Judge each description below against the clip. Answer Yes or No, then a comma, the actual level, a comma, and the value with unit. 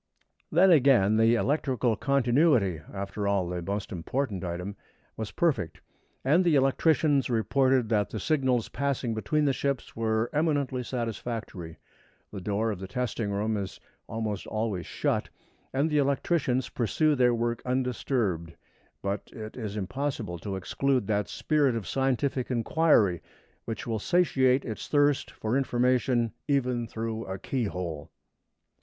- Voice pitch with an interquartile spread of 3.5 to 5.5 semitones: Yes, average, 4.9 semitones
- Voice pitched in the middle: No, low, 120 Hz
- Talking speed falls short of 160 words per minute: Yes, slow, 135 wpm